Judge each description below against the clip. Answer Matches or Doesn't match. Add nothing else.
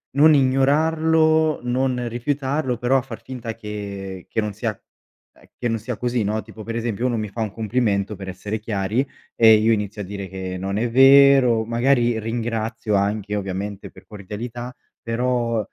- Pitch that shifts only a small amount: Doesn't match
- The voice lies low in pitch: Matches